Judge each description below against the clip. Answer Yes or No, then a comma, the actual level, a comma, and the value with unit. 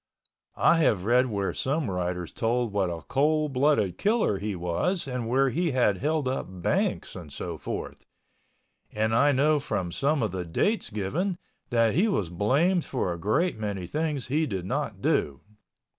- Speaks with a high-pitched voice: No, low, 125 Hz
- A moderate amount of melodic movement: No, wide, 7.8 semitones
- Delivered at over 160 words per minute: Yes, average, 175 wpm